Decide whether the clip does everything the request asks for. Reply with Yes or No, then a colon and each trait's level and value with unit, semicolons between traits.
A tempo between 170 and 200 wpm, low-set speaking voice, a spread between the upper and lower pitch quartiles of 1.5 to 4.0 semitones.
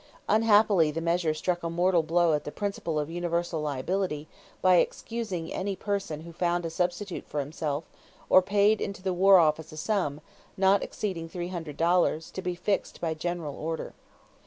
No: average, 175 wpm; medium, 175 Hz; average, 3.0 semitones